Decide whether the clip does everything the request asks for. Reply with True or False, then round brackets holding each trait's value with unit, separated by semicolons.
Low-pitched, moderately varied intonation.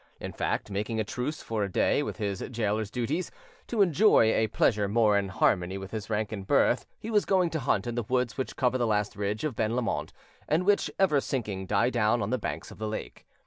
True (110 Hz; 4.0 semitones)